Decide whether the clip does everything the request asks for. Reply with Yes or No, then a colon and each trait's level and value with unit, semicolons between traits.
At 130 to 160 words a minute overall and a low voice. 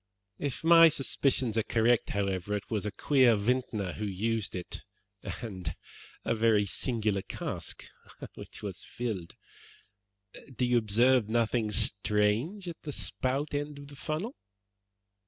Yes: slow, 135 wpm; low, 115 Hz